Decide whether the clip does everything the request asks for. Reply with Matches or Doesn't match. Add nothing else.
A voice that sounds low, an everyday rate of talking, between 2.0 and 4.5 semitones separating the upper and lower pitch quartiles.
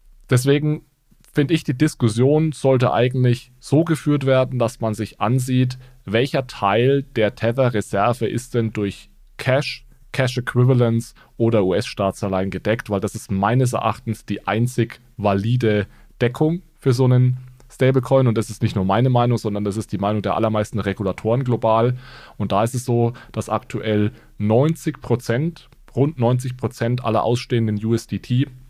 Matches